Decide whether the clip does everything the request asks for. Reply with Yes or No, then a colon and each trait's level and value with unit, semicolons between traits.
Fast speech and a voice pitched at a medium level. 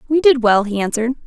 No: fast, 235 wpm; high, 245 Hz